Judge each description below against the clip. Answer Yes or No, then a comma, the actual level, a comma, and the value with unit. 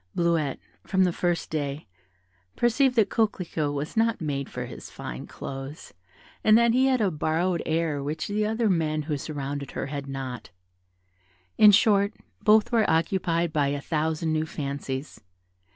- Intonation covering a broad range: Yes, wide, 6.3 semitones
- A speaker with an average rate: Yes, average, 160 wpm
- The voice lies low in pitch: No, medium, 160 Hz